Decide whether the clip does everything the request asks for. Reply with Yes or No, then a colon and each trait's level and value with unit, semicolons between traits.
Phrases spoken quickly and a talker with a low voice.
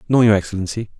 No: average, 180 wpm; low, 105 Hz